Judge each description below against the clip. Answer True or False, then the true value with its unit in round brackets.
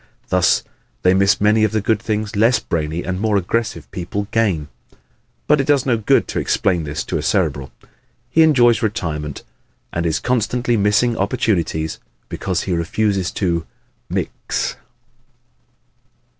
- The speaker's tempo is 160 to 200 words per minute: False (145 wpm)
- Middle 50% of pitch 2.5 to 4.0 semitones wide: False (4.8 semitones)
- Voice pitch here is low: True (100 Hz)